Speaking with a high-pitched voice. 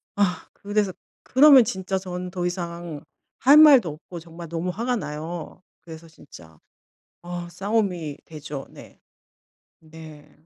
No: medium, 175 Hz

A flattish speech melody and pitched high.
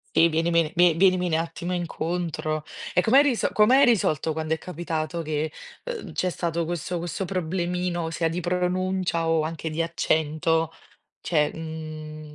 No: narrow, 2.2 semitones; medium, 165 Hz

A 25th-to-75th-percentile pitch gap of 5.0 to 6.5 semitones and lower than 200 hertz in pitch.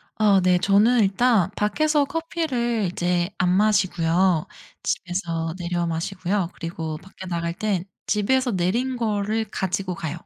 No: average, 4.0 semitones; high, 190 Hz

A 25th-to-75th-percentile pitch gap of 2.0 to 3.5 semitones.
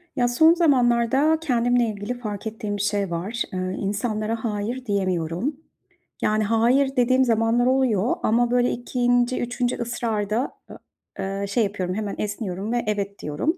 Yes: average, 3.2 semitones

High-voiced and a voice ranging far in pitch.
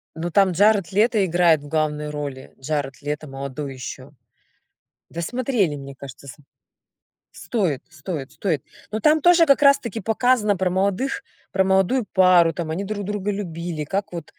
No: medium, 180 Hz; wide, 5.7 semitones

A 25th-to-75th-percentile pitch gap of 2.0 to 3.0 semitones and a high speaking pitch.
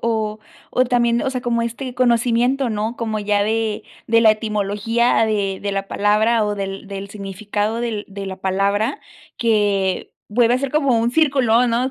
Yes: narrow, 2.6 semitones; high, 220 Hz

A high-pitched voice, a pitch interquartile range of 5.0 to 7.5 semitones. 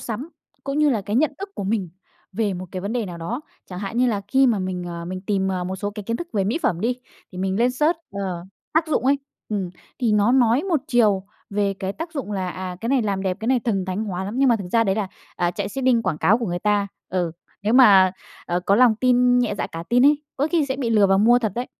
No: high, 210 Hz; average, 4.6 semitones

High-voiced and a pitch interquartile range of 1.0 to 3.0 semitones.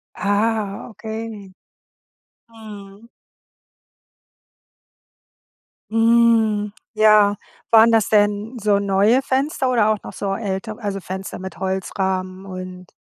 Yes: high, 210 Hz; narrow, 2.4 semitones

